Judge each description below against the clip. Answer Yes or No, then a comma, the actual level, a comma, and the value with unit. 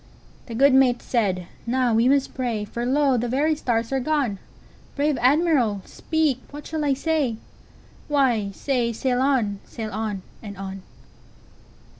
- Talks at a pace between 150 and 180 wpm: No, slow, 135 wpm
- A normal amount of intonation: Yes, average, 4.1 semitones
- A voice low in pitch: No, very high, 250 Hz